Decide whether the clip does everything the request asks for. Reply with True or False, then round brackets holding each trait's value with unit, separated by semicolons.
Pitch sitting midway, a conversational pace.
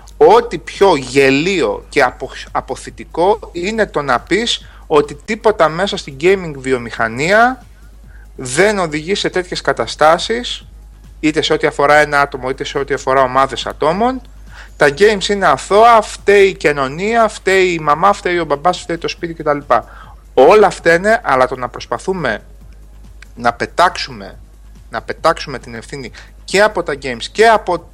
True (175 Hz; 150 wpm)